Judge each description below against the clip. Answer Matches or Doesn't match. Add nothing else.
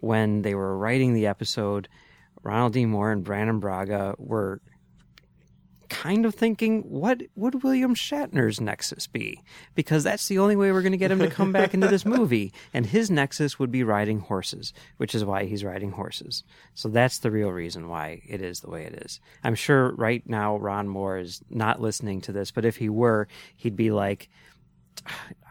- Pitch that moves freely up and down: Matches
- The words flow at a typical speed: Matches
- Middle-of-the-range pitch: Doesn't match